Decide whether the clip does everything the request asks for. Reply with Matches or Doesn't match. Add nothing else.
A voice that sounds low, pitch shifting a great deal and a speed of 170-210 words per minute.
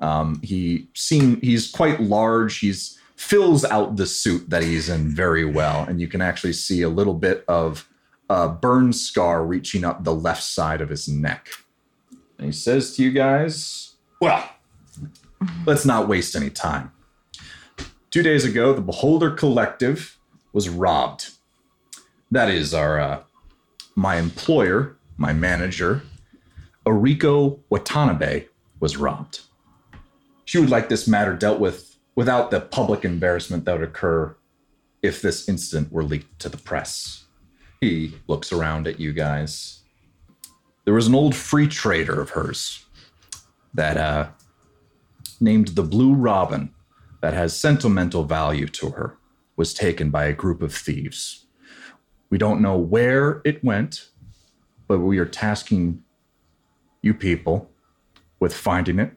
Doesn't match